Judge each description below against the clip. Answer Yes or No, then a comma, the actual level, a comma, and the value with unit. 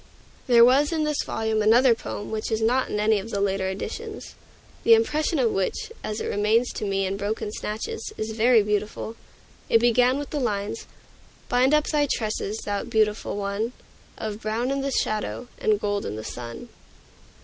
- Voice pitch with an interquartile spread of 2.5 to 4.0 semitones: Yes, average, 3.3 semitones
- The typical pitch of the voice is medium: No, high, 220 Hz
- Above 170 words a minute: Yes, average, 180 wpm